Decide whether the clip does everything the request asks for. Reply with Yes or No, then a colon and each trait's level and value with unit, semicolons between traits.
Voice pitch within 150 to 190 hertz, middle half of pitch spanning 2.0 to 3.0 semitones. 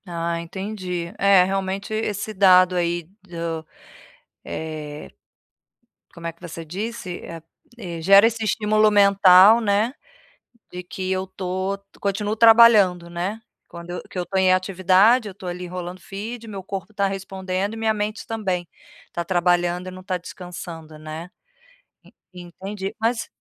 Yes: medium, 185 Hz; average, 2.7 semitones